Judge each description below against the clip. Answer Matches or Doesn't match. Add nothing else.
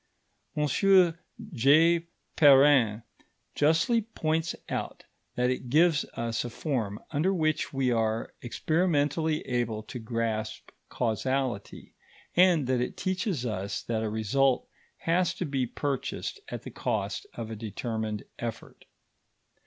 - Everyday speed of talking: Doesn't match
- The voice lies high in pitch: Doesn't match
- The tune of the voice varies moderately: Doesn't match